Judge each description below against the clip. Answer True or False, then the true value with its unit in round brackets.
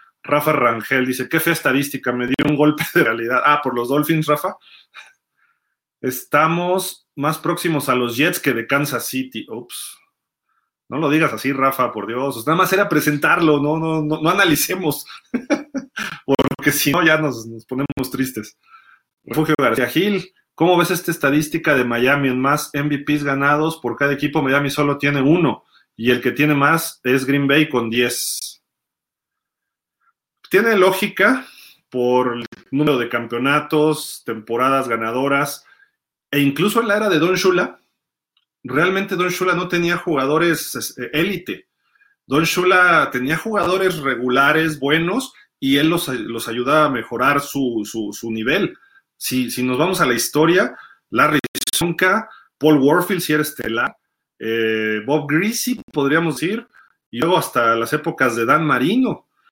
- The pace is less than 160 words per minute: True (150 wpm)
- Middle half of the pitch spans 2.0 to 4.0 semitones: False (4.8 semitones)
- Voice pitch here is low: False (150 Hz)